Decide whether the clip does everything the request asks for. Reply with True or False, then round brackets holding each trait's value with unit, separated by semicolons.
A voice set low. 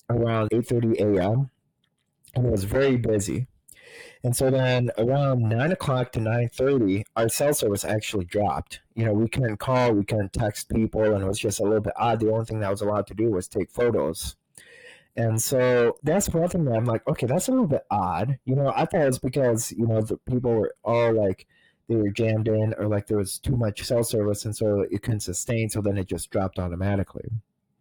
True (115 Hz)